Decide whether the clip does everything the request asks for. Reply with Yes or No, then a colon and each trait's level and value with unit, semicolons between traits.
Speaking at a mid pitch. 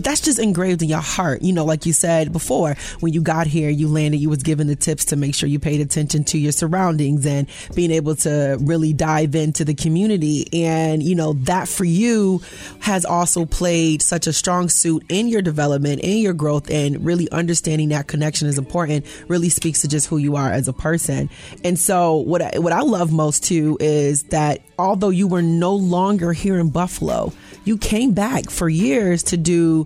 Yes: medium, 160 Hz